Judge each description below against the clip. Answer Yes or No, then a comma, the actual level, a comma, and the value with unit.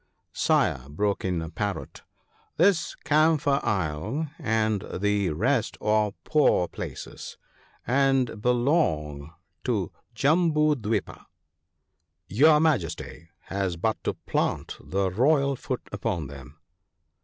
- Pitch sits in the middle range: No, low, 110 Hz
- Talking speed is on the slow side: Yes, slow, 110 wpm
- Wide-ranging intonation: Yes, wide, 7.7 semitones